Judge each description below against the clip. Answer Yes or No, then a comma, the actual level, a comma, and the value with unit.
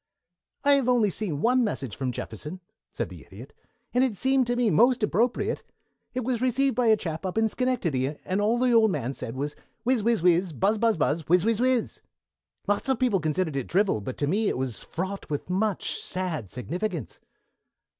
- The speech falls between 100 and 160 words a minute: No, average, 195 wpm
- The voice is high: Yes, high, 205 Hz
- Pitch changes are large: Yes, wide, 7.2 semitones